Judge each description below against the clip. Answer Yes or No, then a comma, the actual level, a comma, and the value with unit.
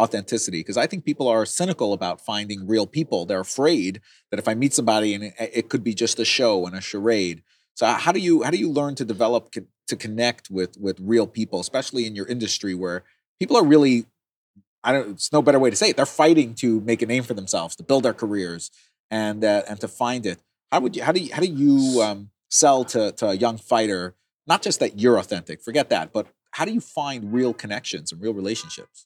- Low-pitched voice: Yes, low, 115 Hz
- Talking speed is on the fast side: Yes, fast, 235 wpm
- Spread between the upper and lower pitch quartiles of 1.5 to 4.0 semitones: No, average, 4.5 semitones